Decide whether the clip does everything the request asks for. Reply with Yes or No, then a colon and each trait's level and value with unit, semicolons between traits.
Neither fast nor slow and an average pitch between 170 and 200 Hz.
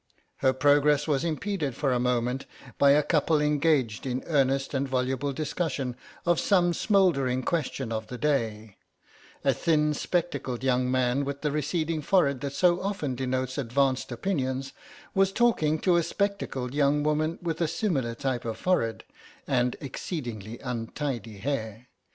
No: average, 150 wpm; medium, 140 Hz